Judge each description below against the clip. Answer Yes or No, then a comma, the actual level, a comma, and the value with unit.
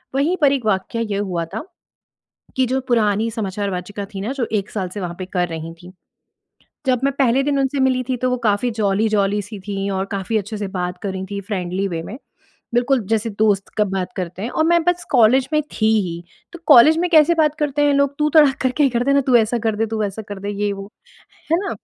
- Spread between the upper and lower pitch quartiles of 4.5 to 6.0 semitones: Yes, average, 5.3 semitones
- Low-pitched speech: No, high, 220 Hz